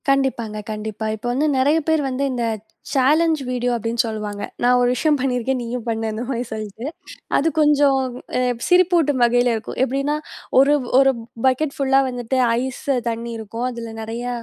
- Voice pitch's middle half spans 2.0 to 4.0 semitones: Yes, average, 3.1 semitones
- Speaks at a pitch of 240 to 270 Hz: Yes, very high, 250 Hz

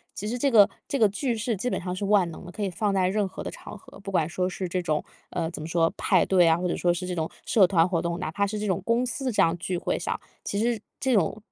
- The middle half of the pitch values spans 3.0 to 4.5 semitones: Yes, average, 3.5 semitones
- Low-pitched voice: No, high, 190 Hz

